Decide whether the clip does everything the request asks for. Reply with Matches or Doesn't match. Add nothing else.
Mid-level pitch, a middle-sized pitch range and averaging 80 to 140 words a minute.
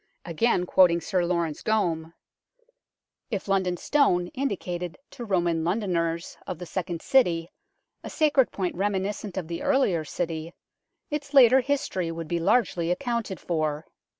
Matches